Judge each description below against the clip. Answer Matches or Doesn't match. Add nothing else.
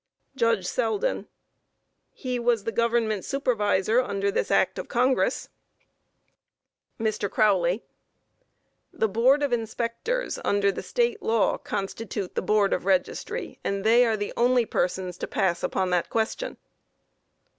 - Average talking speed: Doesn't match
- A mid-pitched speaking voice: Doesn't match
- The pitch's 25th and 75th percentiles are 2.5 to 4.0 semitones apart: Matches